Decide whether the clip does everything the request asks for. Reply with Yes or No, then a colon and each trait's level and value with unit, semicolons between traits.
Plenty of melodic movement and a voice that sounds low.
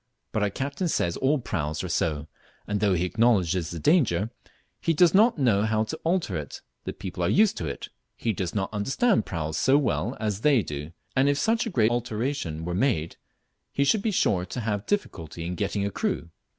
Yes: wide, 8.2 semitones; low, 105 Hz